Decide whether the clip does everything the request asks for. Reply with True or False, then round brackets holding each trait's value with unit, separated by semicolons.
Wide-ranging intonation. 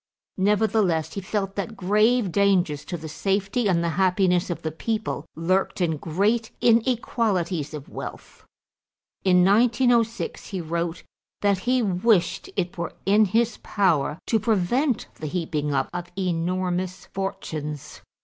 False (4.1 semitones)